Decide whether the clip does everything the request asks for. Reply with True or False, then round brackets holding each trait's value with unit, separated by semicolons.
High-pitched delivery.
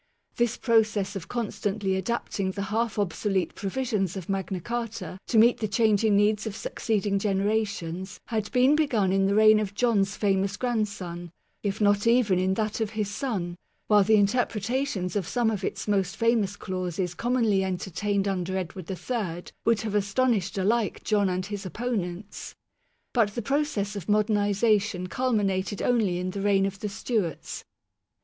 True (205 Hz)